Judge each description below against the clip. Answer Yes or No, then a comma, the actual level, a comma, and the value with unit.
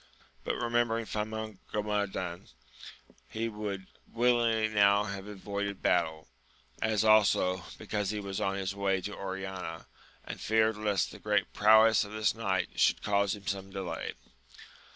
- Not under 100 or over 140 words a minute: Yes, slow, 135 wpm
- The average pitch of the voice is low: Yes, low, 105 Hz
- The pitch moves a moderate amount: No, narrow, 2.0 semitones